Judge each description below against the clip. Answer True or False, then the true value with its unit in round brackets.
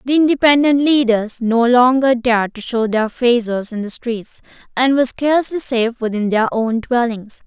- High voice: True (240 Hz)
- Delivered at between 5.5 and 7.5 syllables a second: False (4.9 syllables/s)